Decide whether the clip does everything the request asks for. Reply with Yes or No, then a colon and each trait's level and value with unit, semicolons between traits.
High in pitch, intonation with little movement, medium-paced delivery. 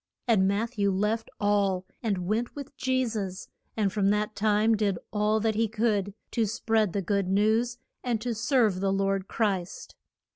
Yes: high, 210 Hz; narrow, 2.3 semitones; average, 175 wpm